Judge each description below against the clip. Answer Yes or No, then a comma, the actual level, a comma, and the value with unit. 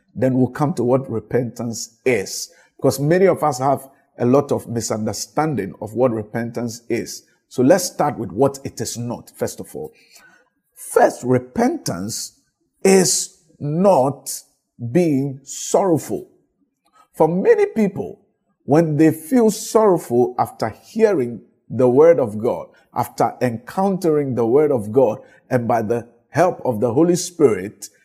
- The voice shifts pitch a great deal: Yes, wide, 7.5 semitones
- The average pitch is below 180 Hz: Yes, medium, 140 Hz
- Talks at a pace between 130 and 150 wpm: Yes, slow, 135 wpm